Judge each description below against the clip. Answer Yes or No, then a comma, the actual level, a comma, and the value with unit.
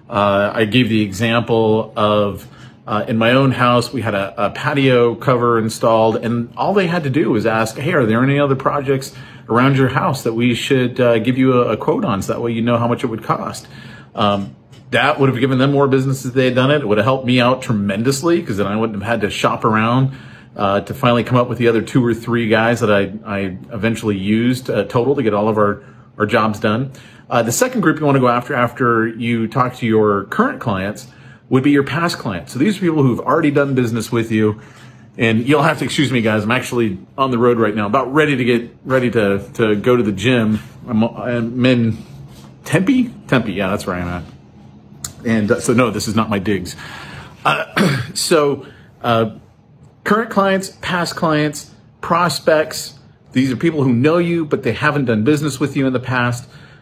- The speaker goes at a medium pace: No, fast, 225 wpm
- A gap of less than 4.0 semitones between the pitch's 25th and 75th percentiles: Yes, average, 3.4 semitones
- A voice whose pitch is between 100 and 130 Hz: Yes, low, 120 Hz